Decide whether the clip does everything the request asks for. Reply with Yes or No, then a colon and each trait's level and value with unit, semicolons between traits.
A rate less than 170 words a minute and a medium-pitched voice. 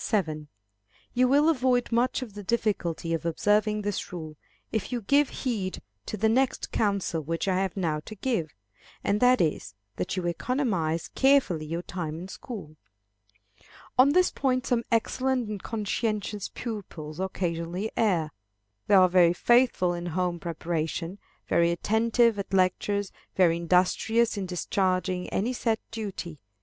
No: average, 145 wpm; high, 195 Hz